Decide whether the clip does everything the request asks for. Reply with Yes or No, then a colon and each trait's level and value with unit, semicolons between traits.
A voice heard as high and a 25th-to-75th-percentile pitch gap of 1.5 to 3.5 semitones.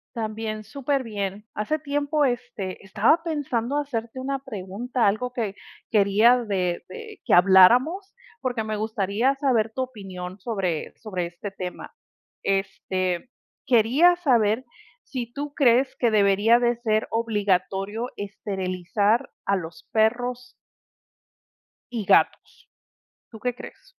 No: high, 225 Hz; average, 4.1 semitones